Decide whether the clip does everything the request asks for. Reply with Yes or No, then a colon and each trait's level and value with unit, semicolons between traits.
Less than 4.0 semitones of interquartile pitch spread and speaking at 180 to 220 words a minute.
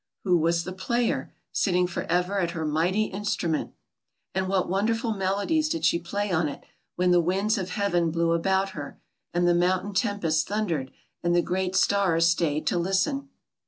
No: average, 2.9 semitones; average, 170 wpm